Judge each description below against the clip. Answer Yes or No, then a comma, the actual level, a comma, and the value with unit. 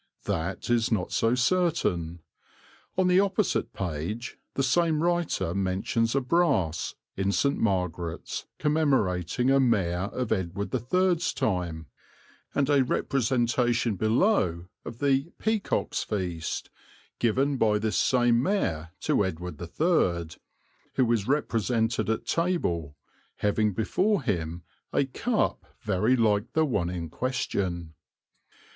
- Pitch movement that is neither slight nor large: No, wide, 7.3 semitones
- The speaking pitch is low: Yes, low, 115 Hz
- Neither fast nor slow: No, slow, 120 wpm